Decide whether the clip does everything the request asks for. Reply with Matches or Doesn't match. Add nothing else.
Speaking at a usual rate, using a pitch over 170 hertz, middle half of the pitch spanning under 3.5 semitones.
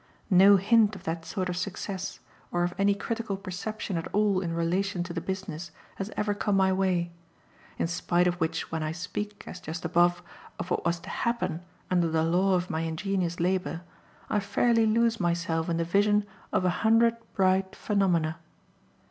Matches